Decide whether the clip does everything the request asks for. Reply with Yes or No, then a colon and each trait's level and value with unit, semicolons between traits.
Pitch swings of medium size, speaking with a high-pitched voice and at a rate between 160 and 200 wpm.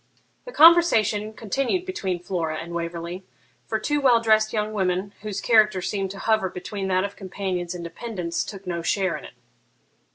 Yes: average, 3.3 semitones; high, 200 Hz; average, 170 wpm